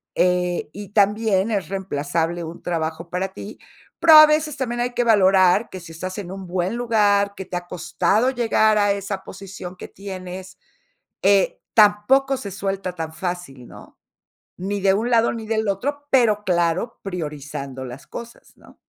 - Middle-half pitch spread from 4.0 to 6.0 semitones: No, average, 3.6 semitones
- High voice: Yes, high, 195 Hz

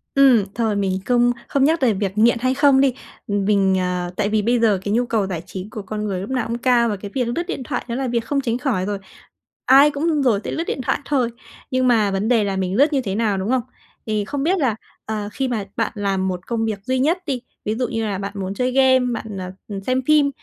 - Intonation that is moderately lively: Yes, average, 4.4 semitones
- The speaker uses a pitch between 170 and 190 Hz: No, high, 230 Hz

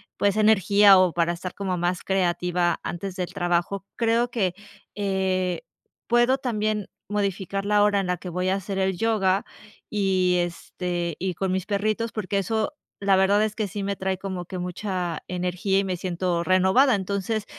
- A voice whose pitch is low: No, high, 190 Hz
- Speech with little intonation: Yes, narrow, 2.2 semitones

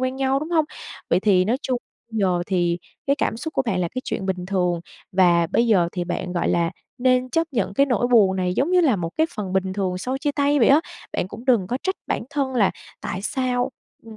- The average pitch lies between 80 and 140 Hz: No, high, 225 Hz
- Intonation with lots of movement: Yes, wide, 6.2 semitones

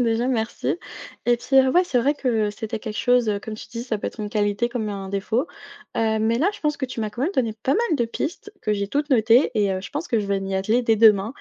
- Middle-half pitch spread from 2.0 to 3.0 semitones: No, average, 3.5 semitones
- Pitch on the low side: No, high, 230 Hz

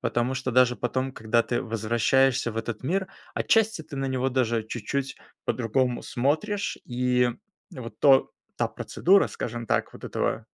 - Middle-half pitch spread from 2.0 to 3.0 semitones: Yes, narrow, 2.5 semitones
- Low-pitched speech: Yes, low, 125 Hz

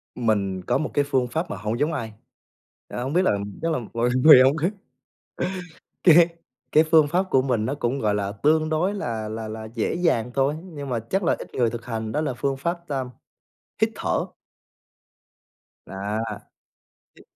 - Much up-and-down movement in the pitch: Yes, wide, 5.9 semitones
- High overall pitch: No, low, 135 Hz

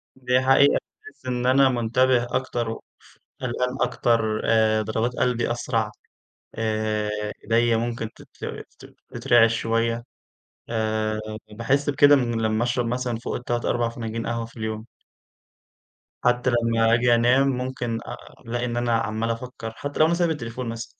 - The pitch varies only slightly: Yes, narrow, 1.8 semitones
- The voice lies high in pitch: No, low, 120 Hz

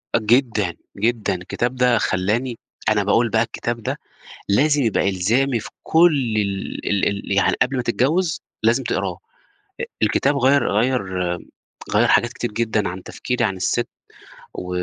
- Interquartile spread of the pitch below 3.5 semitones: No, average, 4.1 semitones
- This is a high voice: No, low, 115 Hz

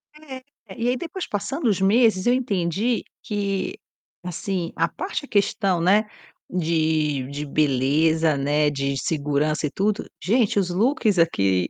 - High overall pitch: No, medium, 180 Hz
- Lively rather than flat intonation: Yes, wide, 6.2 semitones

